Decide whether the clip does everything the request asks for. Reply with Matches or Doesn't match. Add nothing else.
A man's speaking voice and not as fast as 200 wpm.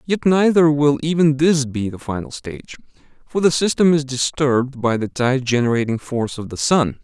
Matches